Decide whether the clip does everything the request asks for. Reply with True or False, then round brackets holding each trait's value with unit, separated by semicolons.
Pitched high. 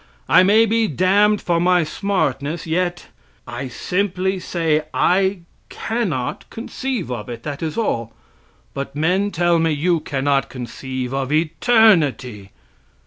False (165 Hz)